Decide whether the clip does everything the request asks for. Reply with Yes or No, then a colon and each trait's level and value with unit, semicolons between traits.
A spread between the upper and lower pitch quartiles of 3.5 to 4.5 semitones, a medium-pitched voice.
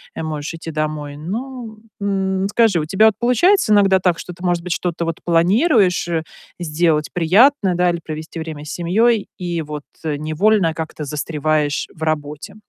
Yes: average, 4.2 semitones; medium, 170 Hz